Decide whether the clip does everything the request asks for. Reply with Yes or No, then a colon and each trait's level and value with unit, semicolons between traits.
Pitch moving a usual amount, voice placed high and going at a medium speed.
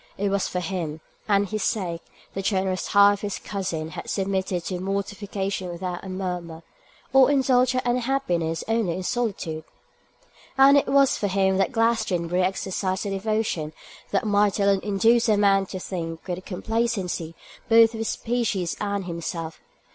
Yes: average, 3.5 semitones; high, 195 Hz; average, 160 wpm